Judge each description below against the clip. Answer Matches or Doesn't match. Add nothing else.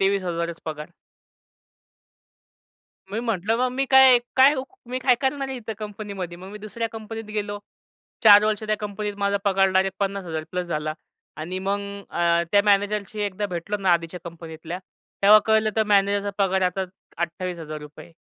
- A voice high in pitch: Matches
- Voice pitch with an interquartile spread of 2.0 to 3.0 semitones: Doesn't match